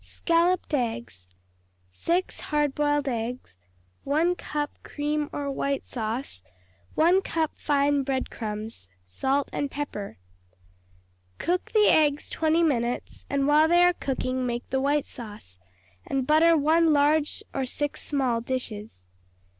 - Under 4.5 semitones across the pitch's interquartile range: Yes, average, 3.9 semitones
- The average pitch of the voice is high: Yes, very high, 280 Hz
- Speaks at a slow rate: Yes, slow, 130 wpm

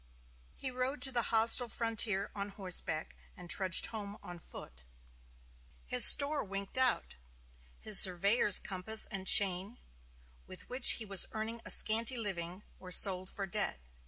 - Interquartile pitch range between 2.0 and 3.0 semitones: No, average, 3.5 semitones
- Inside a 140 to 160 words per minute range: Yes, average, 145 wpm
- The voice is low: No, high, 205 Hz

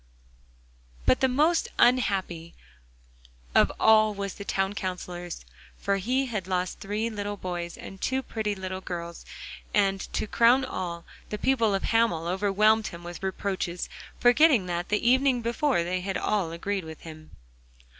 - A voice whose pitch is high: Yes, high, 200 Hz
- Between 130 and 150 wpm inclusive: Yes, average, 145 wpm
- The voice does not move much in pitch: No, average, 4.1 semitones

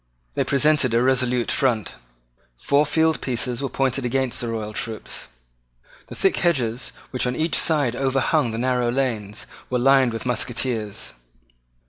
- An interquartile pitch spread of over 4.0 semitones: No, narrow, 2.5 semitones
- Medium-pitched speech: No, low, 125 Hz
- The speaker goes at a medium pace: Yes, average, 145 wpm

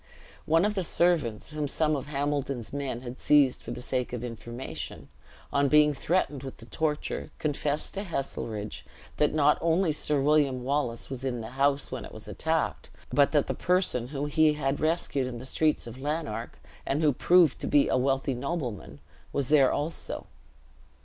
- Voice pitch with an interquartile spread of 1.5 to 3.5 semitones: Yes, average, 3.1 semitones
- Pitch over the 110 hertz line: Yes, medium, 140 Hz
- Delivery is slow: No, average, 180 wpm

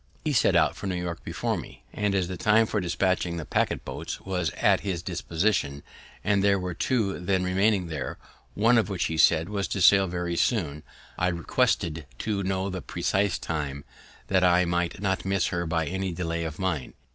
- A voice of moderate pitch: No, very low, 90 Hz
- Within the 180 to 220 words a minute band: Yes, average, 195 wpm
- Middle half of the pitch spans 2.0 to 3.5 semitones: Yes, narrow, 2.6 semitones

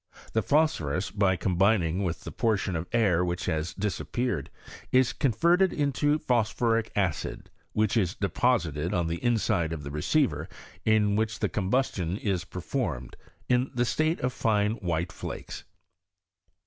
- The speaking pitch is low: Yes, low, 105 Hz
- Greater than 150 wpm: No, average, 140 wpm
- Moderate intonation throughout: No, wide, 5.7 semitones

